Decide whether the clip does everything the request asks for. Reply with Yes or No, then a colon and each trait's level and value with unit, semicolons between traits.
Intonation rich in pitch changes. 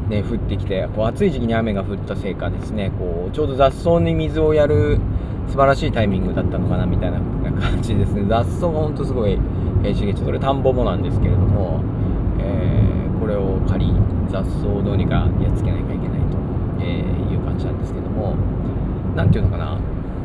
No: average, 3.1 semitones